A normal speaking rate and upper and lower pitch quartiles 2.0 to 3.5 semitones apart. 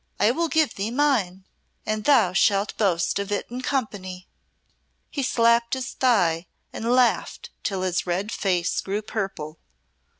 No: average, 145 wpm; average, 4.7 semitones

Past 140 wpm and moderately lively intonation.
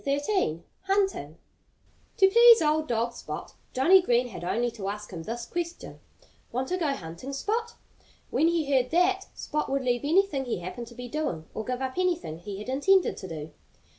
No: average, 185 wpm; wide, 7.3 semitones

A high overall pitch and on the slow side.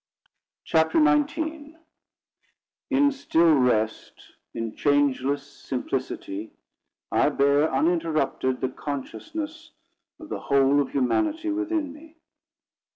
No: medium, 150 Hz; slow, 95 wpm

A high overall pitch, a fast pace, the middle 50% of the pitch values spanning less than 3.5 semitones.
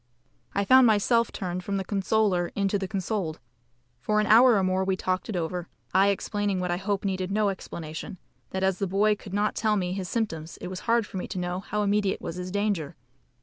Yes: high, 195 Hz; fast, 225 wpm; narrow, 2.4 semitones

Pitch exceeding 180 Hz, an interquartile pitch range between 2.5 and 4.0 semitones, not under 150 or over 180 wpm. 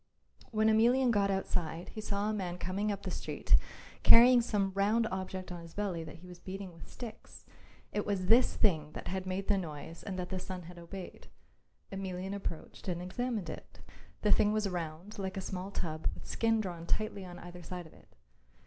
No: high, 190 Hz; average, 2.9 semitones; average, 200 wpm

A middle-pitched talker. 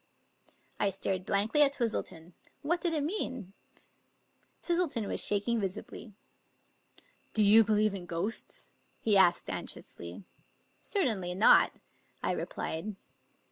No: high, 210 Hz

